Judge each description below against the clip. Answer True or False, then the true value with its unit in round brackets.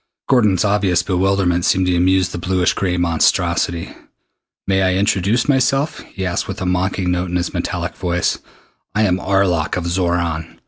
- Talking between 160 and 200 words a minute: True (165 wpm)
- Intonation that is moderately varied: False (1.8 semitones)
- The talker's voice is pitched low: True (90 Hz)